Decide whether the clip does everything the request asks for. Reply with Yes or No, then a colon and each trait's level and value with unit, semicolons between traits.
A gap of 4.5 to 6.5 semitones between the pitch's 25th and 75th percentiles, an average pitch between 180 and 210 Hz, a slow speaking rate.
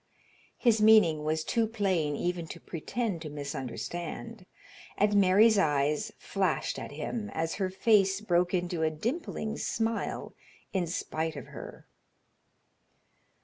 Yes: average, 5.3 semitones; medium, 185 Hz; slow, 125 wpm